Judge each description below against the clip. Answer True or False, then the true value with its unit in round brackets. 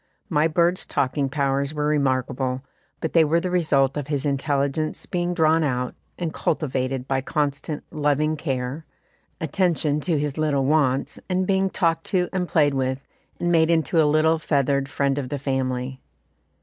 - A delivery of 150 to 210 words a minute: True (160 wpm)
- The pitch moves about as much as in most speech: True (3.0 semitones)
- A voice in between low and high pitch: True (150 Hz)